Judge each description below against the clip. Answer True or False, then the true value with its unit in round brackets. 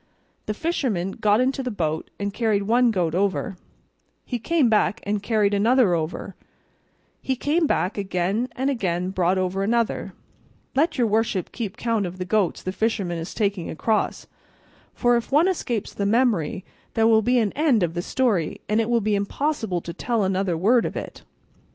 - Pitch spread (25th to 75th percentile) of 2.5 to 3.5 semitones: False (4.3 semitones)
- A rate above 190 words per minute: False (180 wpm)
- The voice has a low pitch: False (210 Hz)